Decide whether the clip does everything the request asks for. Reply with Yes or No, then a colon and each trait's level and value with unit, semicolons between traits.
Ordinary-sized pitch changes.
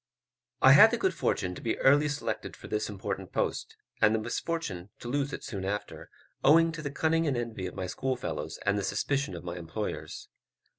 No: wide, 6.9 semitones